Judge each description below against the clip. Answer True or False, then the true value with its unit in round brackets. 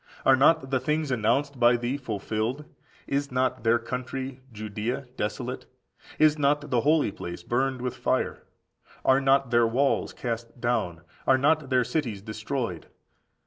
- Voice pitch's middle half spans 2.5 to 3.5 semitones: True (3.1 semitones)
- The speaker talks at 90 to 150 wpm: True (145 wpm)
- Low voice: True (125 Hz)